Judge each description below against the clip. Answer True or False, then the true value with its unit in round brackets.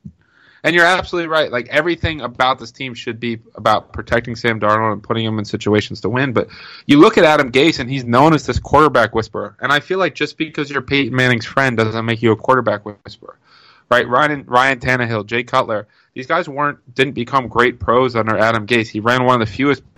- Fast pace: True (220 wpm)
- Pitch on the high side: False (125 Hz)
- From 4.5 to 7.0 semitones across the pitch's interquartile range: False (3.7 semitones)